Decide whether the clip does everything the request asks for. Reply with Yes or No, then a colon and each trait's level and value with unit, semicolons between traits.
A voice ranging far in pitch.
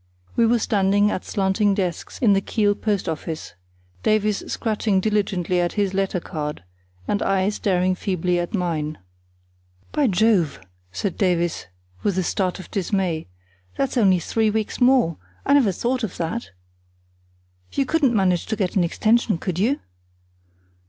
No: average, 3.4 semitones